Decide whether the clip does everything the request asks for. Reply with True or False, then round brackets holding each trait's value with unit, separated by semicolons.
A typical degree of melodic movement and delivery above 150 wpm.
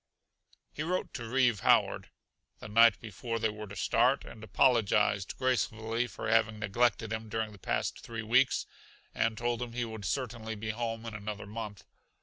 False (1.9 semitones; 170 wpm)